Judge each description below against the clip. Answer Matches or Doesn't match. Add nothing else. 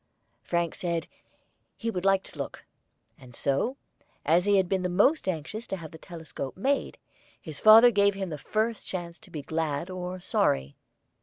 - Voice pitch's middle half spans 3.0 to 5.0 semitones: Matches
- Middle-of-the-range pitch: Matches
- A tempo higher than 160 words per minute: Matches